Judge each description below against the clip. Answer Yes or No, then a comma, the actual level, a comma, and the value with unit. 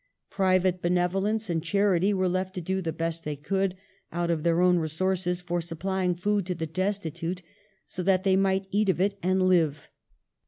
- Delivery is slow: No, average, 190 wpm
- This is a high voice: No, medium, 180 Hz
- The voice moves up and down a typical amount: No, narrow, 1.9 semitones